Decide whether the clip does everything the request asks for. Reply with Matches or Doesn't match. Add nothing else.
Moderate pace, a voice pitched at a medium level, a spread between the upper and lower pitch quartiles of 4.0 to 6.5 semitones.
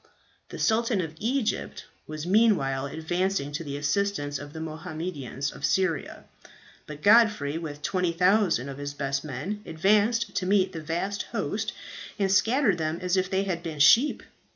Matches